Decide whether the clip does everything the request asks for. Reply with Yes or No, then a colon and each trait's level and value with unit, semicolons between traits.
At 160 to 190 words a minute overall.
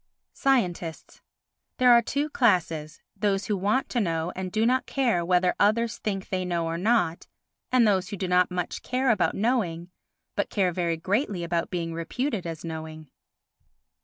Yes: average, 165 wpm